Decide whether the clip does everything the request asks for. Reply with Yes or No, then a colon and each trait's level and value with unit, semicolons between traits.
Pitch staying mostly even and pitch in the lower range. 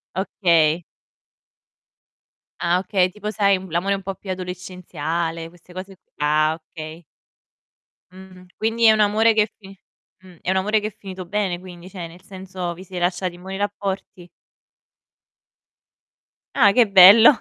No: narrow, 2.3 semitones; medium, 185 Hz